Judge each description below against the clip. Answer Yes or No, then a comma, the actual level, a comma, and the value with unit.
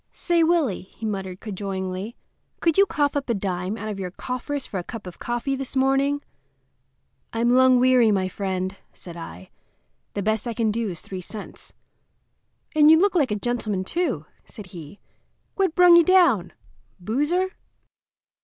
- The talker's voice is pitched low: No, high, 230 Hz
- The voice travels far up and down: Yes, wide, 7.0 semitones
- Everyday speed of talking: Yes, average, 165 wpm